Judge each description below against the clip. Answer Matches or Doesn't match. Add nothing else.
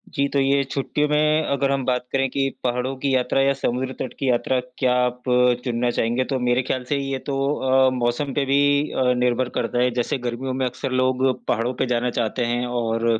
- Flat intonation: Matches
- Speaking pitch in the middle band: Doesn't match